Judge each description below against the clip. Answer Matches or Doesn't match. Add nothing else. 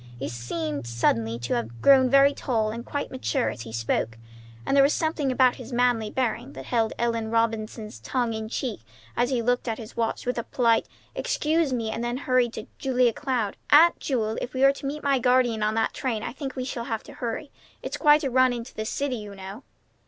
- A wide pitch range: Doesn't match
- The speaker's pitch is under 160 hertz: Doesn't match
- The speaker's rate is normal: Doesn't match